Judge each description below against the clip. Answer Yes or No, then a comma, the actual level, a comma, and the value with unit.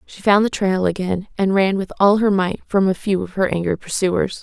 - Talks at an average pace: No, fast, 245 wpm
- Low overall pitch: No, high, 190 Hz